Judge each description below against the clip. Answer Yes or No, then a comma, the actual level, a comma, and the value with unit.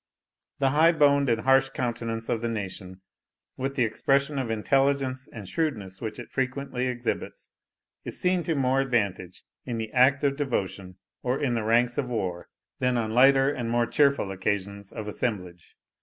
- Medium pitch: No, low, 125 Hz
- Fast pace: No, average, 170 wpm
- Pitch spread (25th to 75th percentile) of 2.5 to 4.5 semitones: Yes, average, 4.0 semitones